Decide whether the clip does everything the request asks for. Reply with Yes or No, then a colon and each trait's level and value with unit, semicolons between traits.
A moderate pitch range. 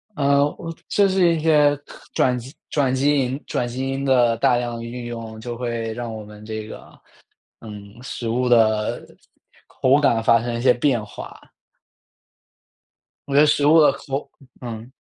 Yes: average, 3.3 semitones